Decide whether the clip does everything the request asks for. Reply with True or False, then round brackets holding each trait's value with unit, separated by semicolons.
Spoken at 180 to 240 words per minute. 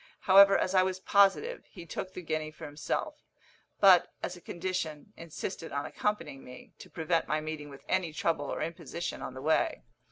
True (185 wpm)